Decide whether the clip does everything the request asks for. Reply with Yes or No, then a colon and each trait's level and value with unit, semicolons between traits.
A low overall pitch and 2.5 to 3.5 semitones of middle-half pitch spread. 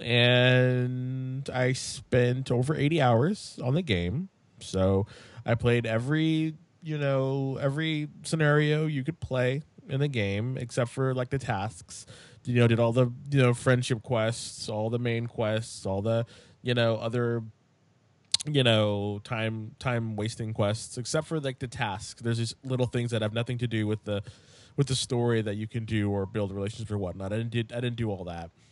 Yes: low, 120 Hz; average, 3.1 semitones